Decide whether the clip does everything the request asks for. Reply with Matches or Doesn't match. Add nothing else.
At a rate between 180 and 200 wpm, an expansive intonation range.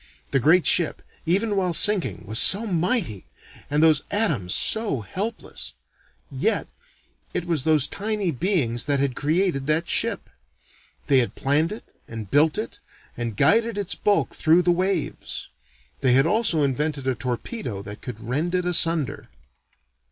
Doesn't match